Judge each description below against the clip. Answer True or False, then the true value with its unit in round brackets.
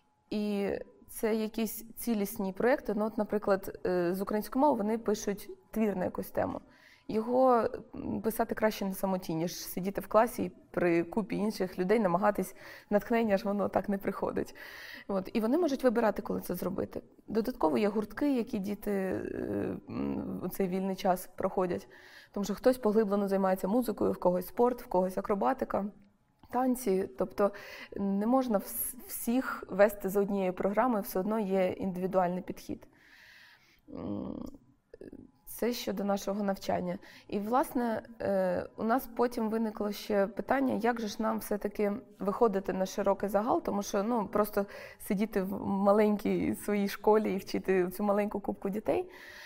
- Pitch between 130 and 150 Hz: False (205 Hz)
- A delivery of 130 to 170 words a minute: True (140 wpm)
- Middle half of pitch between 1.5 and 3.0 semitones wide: True (2.5 semitones)